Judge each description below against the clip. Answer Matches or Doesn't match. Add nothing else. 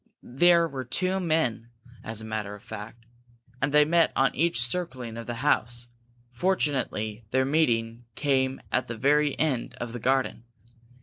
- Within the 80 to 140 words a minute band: Doesn't match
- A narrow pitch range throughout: Doesn't match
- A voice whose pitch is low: Matches